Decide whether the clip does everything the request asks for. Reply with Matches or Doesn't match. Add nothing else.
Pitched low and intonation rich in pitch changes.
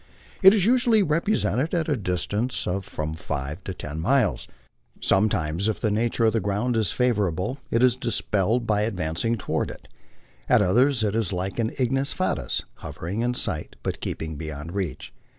Matches